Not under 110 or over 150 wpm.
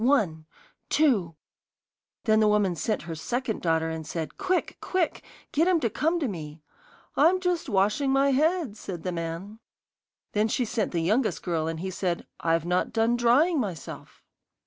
No: average, 170 wpm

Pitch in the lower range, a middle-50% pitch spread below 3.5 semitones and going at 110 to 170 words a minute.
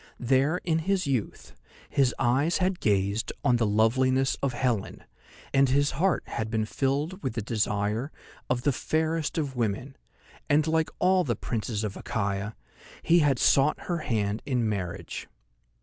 No: low, 130 Hz; wide, 5.4 semitones; average, 155 wpm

